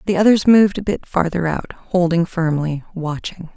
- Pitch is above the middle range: No, medium, 175 Hz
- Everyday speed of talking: Yes, average, 170 wpm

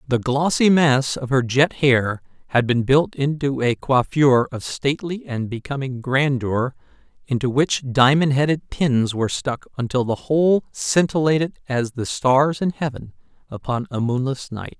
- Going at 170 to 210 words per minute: No, average, 155 wpm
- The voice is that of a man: Yes, male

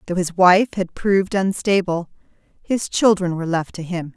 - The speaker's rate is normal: Yes, average, 175 wpm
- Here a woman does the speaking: Yes, female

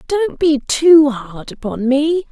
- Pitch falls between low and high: No, very high, 290 Hz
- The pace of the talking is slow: No, average, 155 wpm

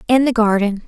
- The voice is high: Yes, high, 225 Hz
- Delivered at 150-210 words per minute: Yes, fast, 205 wpm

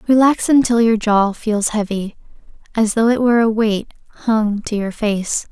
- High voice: Yes, high, 220 Hz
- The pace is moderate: Yes, average, 175 wpm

